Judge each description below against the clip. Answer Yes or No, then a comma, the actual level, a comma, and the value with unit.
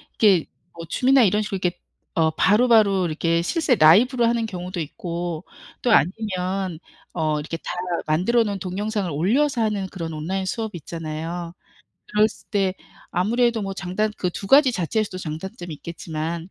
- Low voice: No, medium, 185 Hz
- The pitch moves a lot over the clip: No, average, 4.5 semitones